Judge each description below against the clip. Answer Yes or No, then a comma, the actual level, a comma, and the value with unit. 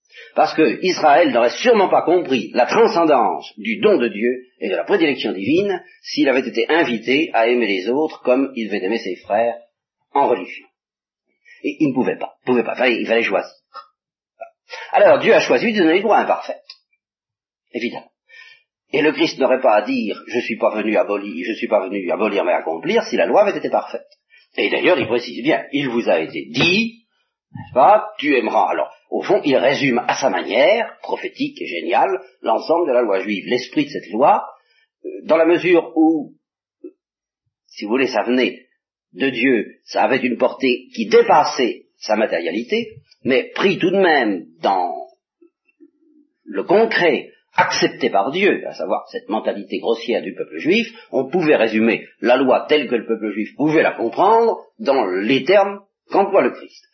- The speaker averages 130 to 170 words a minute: No, average, 180 wpm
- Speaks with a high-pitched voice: Yes, high, 230 Hz